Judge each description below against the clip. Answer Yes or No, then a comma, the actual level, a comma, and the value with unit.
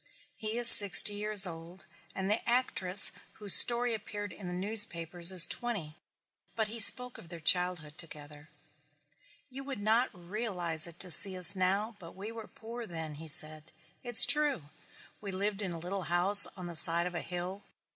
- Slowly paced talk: No, average, 175 wpm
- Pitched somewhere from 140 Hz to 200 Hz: Yes, high, 190 Hz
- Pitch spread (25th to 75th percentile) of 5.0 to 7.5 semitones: No, average, 4.0 semitones